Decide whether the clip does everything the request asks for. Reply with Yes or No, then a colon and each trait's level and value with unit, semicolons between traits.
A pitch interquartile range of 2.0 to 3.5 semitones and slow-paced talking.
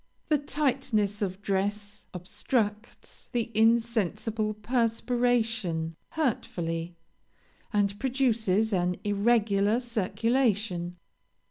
Yes: average, 3.0 semitones; slow, 75 wpm